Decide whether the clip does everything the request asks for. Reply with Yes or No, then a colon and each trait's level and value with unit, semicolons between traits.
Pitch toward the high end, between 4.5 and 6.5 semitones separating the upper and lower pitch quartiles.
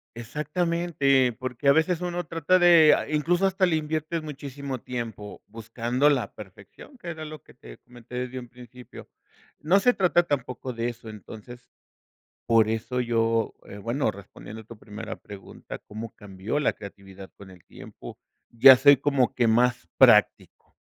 No: low, 125 Hz; average, 5.3 semitones